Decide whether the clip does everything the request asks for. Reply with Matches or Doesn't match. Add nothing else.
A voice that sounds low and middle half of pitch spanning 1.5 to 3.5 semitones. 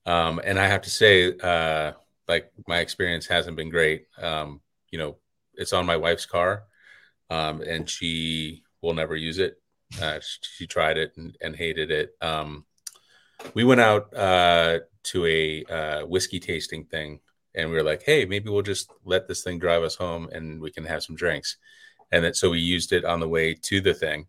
Matches